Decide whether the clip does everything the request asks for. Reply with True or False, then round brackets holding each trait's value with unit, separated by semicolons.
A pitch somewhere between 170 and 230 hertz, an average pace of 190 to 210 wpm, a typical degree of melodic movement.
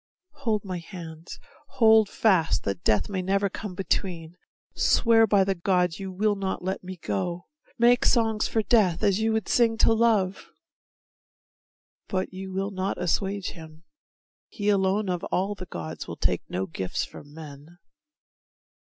False (190 Hz; 155 wpm; 3.6 semitones)